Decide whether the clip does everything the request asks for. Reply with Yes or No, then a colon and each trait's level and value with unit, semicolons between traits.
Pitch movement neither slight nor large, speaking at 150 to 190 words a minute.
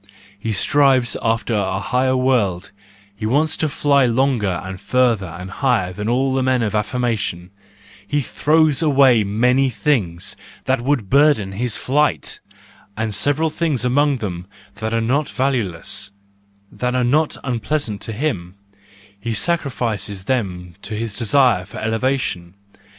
No: average, 5.0 semitones; slow, 135 wpm